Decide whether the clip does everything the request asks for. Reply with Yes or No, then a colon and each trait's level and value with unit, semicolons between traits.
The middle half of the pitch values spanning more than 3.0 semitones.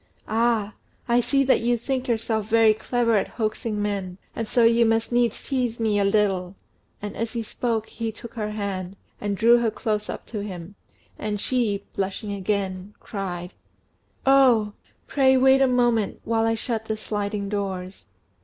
No: average, 2.7 semitones